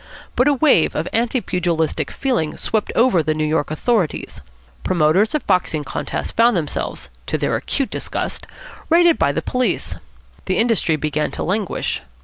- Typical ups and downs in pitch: No, wide, 7.6 semitones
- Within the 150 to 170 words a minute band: Yes, average, 155 wpm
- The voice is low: No, medium, 185 Hz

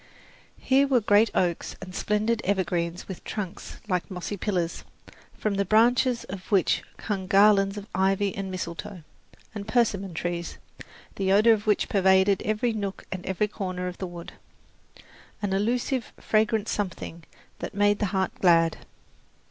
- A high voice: Yes, high, 195 Hz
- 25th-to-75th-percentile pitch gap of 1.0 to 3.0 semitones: Yes, narrow, 2.5 semitones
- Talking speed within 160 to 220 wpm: No, average, 145 wpm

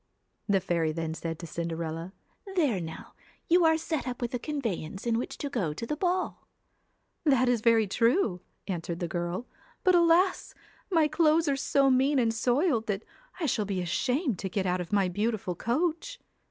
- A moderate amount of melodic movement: No, wide, 9.0 semitones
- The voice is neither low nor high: No, high, 230 Hz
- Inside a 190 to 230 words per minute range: Yes, average, 195 wpm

